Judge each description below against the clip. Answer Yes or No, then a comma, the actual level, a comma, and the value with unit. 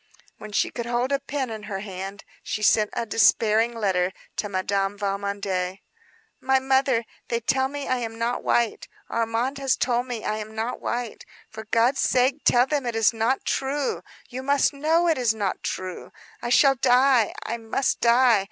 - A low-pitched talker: No, high, 235 Hz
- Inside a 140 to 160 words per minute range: No, average, 180 wpm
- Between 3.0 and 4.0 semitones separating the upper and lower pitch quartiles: Yes, average, 3.6 semitones